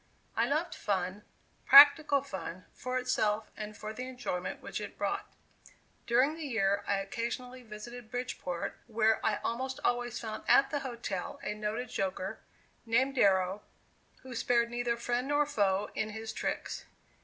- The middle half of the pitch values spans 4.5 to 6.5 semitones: No, average, 3.4 semitones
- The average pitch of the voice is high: Yes, high, 235 Hz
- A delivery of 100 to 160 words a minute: Yes, average, 150 wpm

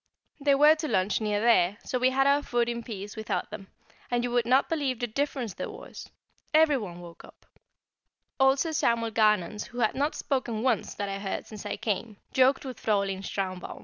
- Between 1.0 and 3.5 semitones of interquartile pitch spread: No, average, 4.4 semitones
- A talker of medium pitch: No, high, 235 Hz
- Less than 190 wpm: No, average, 200 wpm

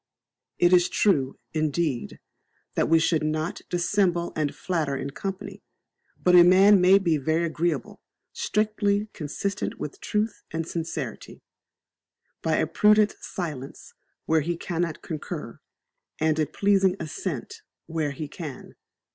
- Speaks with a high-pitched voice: No, medium, 170 Hz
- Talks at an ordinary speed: No, slow, 130 wpm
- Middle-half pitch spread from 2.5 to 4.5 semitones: Yes, average, 3.7 semitones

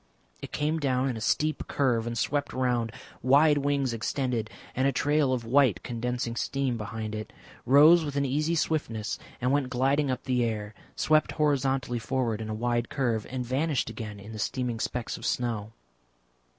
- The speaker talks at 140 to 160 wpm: No, average, 175 wpm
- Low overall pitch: Yes, low, 125 Hz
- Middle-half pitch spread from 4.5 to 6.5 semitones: No, average, 3.5 semitones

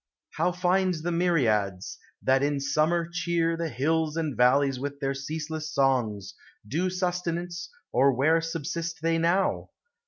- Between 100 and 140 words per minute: Yes, slow, 135 wpm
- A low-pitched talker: No, medium, 160 Hz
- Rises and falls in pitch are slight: No, average, 3.8 semitones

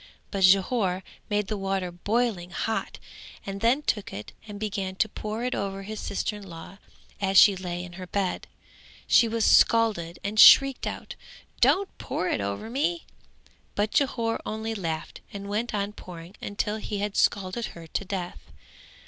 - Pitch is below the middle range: No, high, 200 Hz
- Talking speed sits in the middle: Yes, average, 165 wpm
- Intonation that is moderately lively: Yes, average, 3.0 semitones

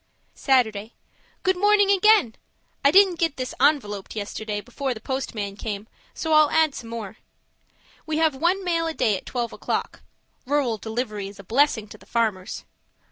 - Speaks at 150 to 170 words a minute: Yes, average, 165 wpm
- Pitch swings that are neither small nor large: No, wide, 6.8 semitones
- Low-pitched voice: No, very high, 250 Hz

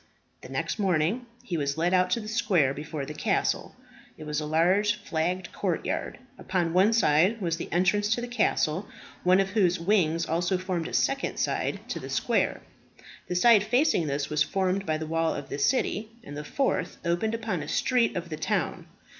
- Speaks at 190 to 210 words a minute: Yes, average, 195 wpm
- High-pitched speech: No, medium, 180 Hz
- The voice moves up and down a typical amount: Yes, average, 4.8 semitones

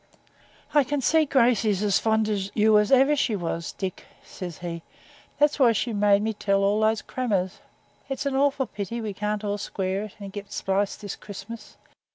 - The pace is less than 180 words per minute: No, average, 190 wpm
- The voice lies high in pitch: Yes, high, 210 Hz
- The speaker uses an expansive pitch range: No, average, 3.4 semitones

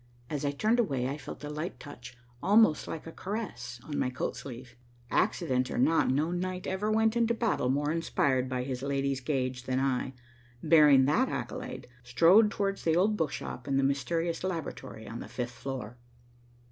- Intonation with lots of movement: Yes, wide, 6.0 semitones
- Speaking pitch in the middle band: Yes, medium, 145 Hz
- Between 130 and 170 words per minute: No, average, 185 wpm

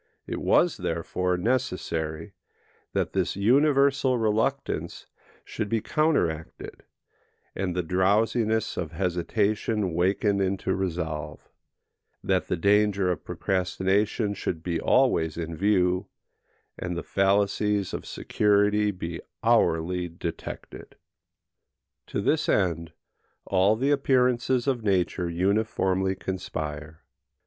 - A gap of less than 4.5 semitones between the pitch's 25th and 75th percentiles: Yes, average, 3.6 semitones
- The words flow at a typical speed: No, slow, 105 wpm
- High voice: No, very low, 95 Hz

